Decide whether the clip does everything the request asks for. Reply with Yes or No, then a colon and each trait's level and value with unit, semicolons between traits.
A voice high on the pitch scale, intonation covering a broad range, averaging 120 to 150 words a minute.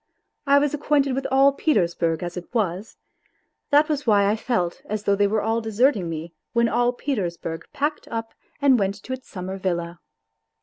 No: high, 220 Hz; wide, 6.9 semitones; average, 185 wpm